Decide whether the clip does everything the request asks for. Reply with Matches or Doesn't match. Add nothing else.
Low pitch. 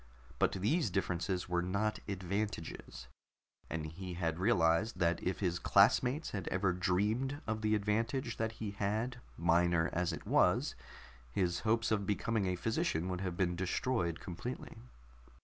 Matches